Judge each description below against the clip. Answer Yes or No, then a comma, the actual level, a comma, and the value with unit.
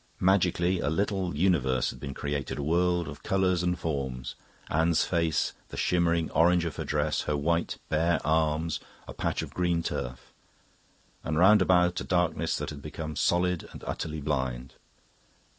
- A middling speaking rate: Yes, average, 160 wpm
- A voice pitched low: Yes, very low, 80 Hz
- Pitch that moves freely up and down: No, average, 3.2 semitones